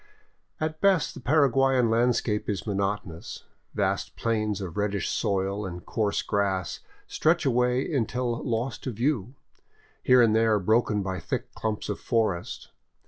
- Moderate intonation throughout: Yes, average, 3.7 semitones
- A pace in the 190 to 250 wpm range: No, average, 140 wpm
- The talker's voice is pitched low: Yes, low, 110 Hz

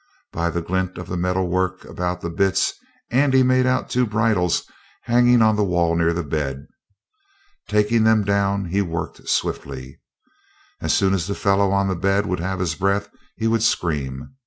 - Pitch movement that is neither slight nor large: Yes, average, 3.5 semitones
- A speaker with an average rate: Yes, average, 180 wpm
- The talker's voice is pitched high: No, very low, 95 Hz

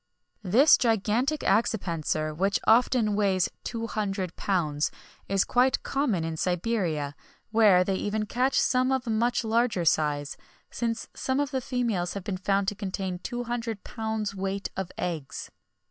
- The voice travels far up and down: No, average, 4.4 semitones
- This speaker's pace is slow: No, average, 160 wpm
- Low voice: No, high, 205 Hz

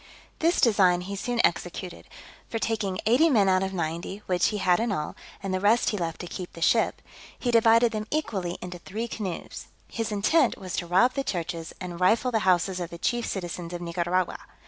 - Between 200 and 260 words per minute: Yes, fast, 205 wpm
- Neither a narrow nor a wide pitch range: Yes, average, 4.3 semitones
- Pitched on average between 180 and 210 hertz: Yes, high, 190 Hz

